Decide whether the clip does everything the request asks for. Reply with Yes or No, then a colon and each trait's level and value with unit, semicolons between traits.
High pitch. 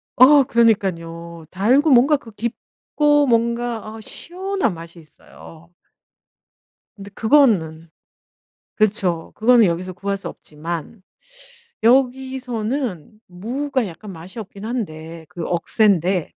Yes: high, 215 Hz